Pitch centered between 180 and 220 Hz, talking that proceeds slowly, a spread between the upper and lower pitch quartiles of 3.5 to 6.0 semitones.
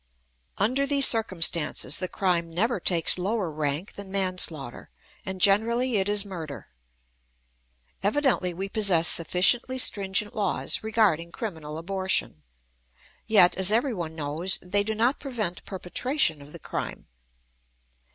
Yes: high, 190 Hz; slow, 120 wpm; average, 4.4 semitones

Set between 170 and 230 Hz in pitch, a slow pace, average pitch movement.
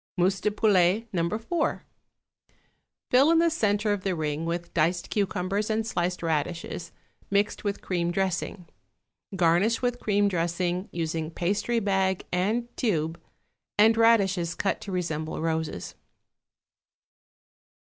Yes: medium, 185 Hz; slow, 125 wpm; average, 3.6 semitones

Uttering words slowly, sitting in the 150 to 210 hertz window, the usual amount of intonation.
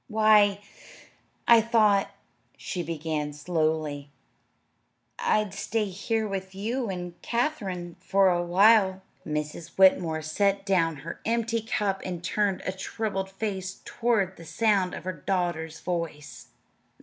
Yes: slow, 120 wpm; high, 190 Hz; average, 3.9 semitones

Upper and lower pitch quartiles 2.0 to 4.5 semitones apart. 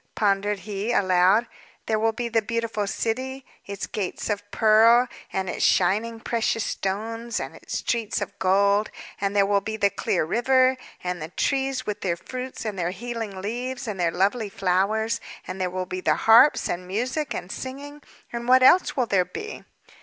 Yes: average, 3.6 semitones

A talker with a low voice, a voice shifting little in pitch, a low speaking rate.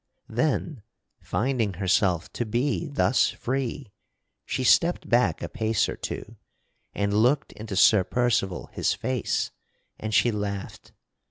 No: low, 115 Hz; average, 4.2 semitones; slow, 125 wpm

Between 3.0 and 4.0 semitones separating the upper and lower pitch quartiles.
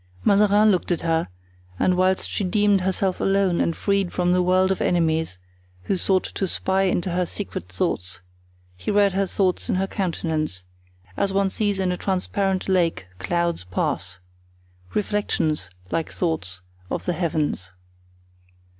Yes: average, 3.5 semitones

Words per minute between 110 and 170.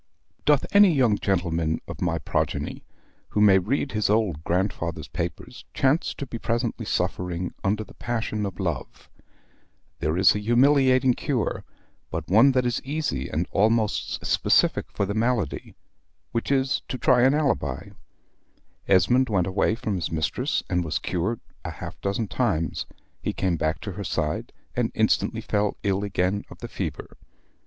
Yes: average, 160 wpm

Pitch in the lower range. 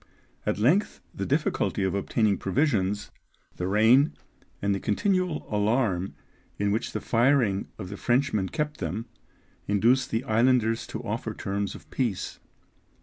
Yes: low, 110 Hz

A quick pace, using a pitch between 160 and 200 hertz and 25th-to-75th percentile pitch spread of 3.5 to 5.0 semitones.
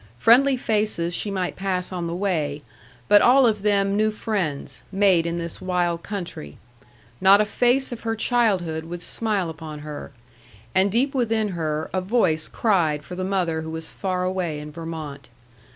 No: average, 170 wpm; medium, 185 Hz; average, 4.5 semitones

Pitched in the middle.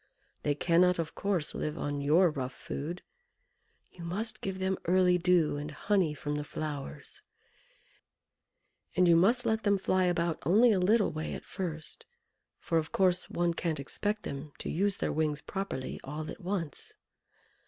Yes: medium, 175 Hz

